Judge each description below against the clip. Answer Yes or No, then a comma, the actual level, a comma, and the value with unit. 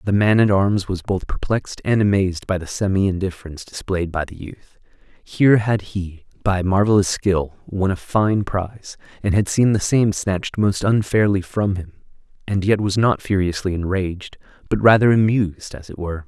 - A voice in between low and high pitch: No, very low, 95 Hz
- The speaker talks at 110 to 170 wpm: No, average, 180 wpm